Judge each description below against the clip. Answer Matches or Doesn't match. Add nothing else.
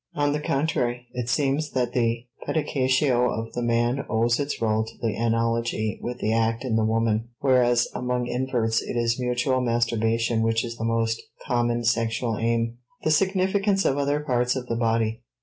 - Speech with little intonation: Matches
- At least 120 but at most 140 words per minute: Doesn't match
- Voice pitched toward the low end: Matches